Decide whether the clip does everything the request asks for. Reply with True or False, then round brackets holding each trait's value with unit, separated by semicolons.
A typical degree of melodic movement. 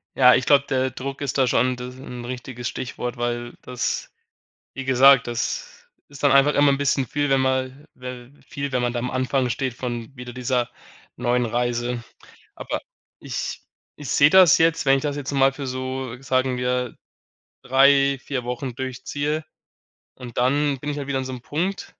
False (1.9 semitones)